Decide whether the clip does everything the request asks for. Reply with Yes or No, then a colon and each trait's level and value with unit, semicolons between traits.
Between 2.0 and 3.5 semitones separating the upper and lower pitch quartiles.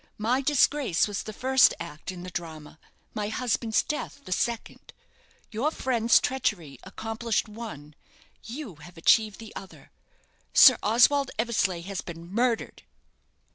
No: average, 5.2 semitones